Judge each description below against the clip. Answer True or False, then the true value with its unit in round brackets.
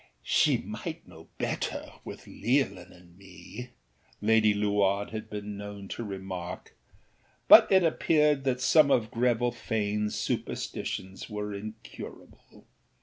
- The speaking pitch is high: False (105 Hz)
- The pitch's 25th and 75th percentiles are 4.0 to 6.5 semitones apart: False (3.5 semitones)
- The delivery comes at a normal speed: False (120 wpm)